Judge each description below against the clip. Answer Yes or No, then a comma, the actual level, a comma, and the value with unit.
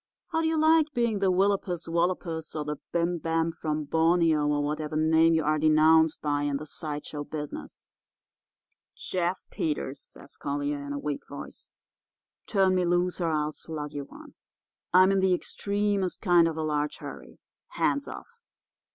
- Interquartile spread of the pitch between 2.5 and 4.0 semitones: Yes, average, 3.5 semitones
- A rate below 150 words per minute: No, average, 170 wpm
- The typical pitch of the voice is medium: Yes, medium, 160 Hz